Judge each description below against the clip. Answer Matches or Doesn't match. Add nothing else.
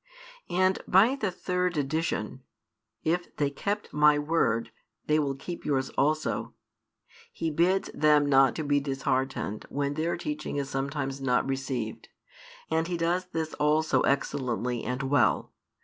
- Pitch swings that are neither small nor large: Matches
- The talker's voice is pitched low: Doesn't match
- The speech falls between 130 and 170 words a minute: Matches